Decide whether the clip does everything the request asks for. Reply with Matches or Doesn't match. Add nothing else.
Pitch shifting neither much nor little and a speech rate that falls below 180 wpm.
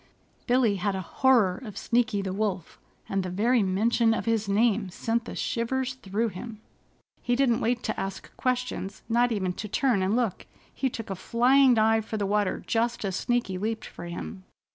Doesn't match